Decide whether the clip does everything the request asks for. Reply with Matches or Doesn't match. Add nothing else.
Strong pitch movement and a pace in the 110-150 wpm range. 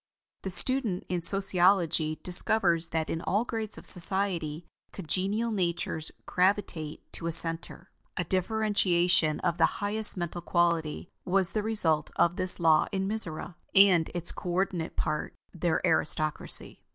Doesn't match